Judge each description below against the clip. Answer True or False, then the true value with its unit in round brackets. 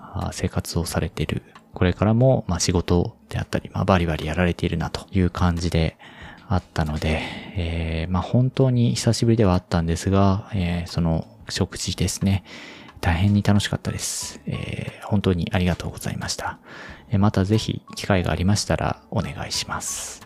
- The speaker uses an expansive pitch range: False (3.6 semitones)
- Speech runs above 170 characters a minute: True (340 characters per minute)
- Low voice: True (90 Hz)